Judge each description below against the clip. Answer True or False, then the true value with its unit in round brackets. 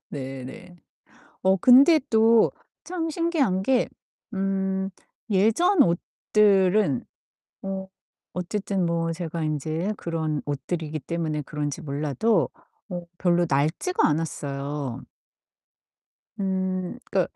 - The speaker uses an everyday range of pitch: True (4.8 semitones)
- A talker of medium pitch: True (180 Hz)